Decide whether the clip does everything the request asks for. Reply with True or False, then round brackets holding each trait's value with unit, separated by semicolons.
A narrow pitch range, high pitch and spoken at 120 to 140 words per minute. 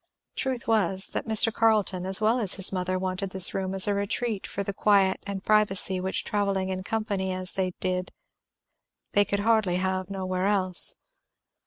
False (1.9 semitones; 195 Hz; 170 wpm)